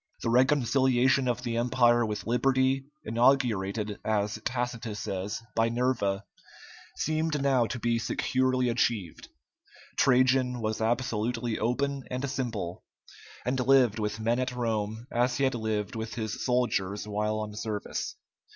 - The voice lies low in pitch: Yes, low, 120 Hz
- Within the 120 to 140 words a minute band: Yes, slow, 135 wpm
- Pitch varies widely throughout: No, average, 2.9 semitones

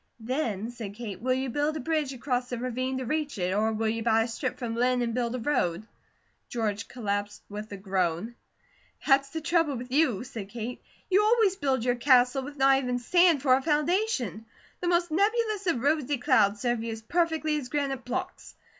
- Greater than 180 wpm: Yes, average, 200 wpm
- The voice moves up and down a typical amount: Yes, average, 4.8 semitones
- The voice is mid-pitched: No, very high, 255 Hz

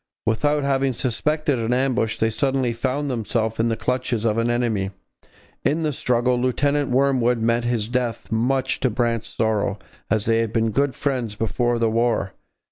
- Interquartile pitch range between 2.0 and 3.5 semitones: Yes, average, 2.7 semitones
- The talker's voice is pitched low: Yes, low, 120 Hz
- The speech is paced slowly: No, average, 170 wpm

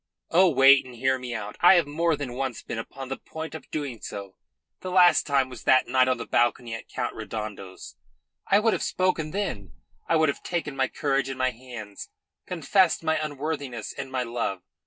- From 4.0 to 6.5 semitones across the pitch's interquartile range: Yes, average, 4.7 semitones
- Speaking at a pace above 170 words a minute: Yes, average, 200 wpm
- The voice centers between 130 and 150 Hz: Yes, low, 135 Hz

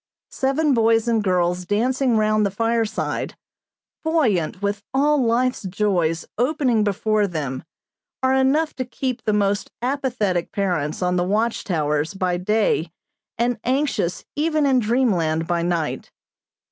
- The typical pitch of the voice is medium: No, high, 215 Hz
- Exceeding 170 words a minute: No, slow, 135 wpm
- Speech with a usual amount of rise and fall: No, wide, 6.0 semitones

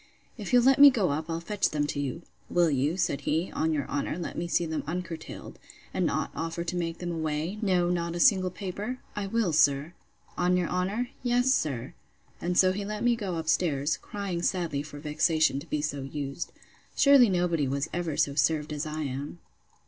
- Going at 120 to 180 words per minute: No, average, 200 wpm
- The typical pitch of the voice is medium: Yes, medium, 170 Hz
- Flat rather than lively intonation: No, average, 3.7 semitones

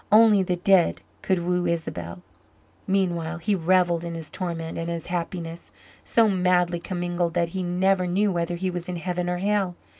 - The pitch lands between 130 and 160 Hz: No, medium, 175 Hz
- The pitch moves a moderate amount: No, narrow, 1.6 semitones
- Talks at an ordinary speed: Yes, average, 175 wpm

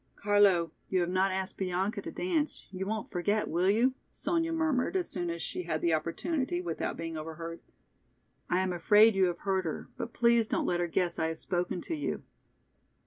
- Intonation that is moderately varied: Yes, average, 4.3 semitones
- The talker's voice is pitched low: No, high, 190 Hz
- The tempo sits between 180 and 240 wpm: Yes, average, 195 wpm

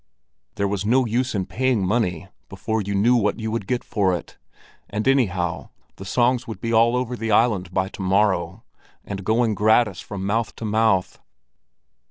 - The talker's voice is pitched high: No, low, 105 Hz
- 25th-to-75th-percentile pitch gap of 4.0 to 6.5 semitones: No, average, 3.3 semitones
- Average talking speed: Yes, average, 180 wpm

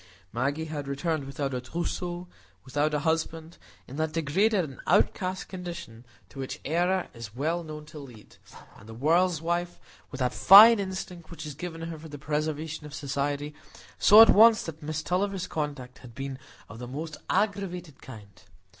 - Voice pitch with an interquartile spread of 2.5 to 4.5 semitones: Yes, average, 4.0 semitones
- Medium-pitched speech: Yes, medium, 155 Hz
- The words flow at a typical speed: Yes, average, 170 wpm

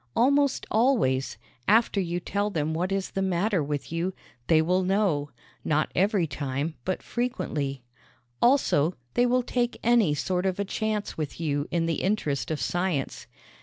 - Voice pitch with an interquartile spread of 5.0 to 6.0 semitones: Yes, wide, 5.6 semitones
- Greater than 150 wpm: Yes, average, 160 wpm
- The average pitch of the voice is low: No, medium, 185 Hz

